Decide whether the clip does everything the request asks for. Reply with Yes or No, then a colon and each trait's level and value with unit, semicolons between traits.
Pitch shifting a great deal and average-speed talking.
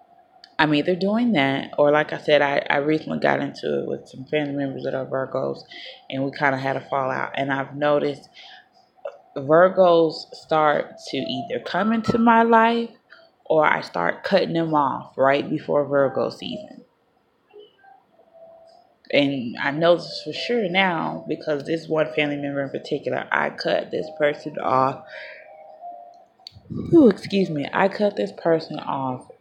Yes: wide, 8.3 semitones; average, 155 wpm